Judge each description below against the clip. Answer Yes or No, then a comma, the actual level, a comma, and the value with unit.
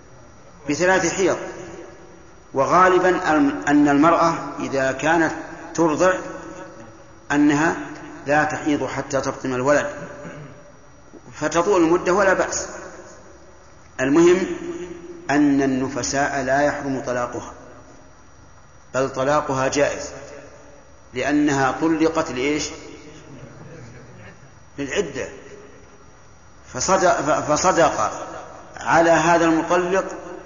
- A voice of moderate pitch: Yes, medium, 150 Hz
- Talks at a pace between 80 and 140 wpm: No, average, 70 wpm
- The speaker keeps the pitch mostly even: No, average, 4.3 semitones